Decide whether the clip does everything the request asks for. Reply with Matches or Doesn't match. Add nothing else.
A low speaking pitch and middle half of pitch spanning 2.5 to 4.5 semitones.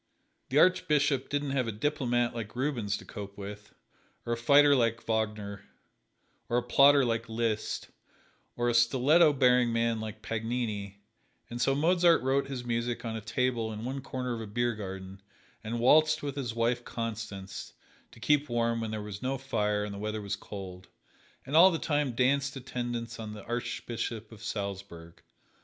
Matches